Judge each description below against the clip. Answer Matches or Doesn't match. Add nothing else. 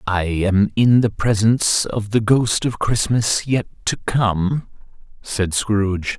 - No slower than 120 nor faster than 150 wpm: Matches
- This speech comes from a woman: Doesn't match